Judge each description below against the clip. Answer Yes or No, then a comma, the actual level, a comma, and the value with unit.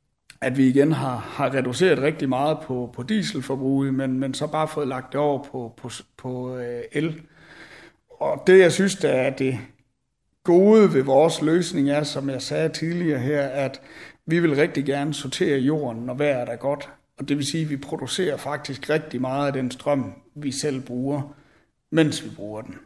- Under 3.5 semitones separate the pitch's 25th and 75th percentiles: Yes, average, 2.7 semitones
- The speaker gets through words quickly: No, average, 175 wpm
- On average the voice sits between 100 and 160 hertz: Yes, medium, 140 Hz